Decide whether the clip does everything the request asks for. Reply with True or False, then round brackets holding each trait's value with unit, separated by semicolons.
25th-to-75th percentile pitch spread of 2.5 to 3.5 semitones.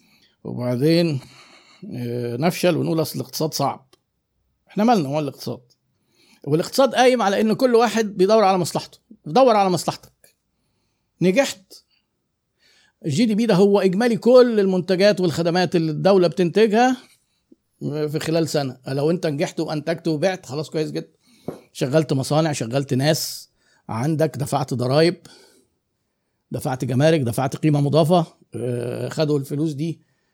False (4.5 semitones)